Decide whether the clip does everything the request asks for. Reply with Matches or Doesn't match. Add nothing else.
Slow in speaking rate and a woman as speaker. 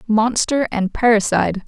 Matches